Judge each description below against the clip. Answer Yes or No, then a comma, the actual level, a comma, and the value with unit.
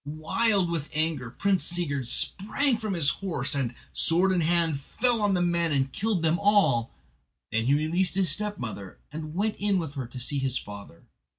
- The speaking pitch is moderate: Yes, medium, 165 Hz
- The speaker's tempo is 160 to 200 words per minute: Yes, average, 185 wpm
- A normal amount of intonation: No, wide, 5.9 semitones